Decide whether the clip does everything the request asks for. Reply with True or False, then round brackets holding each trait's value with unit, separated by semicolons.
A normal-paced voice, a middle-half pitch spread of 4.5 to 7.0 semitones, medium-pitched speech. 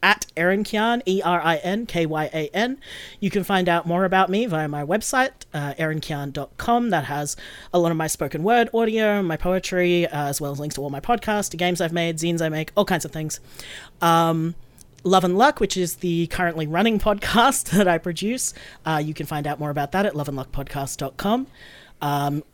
False (210 wpm; 5.1 semitones; 170 Hz)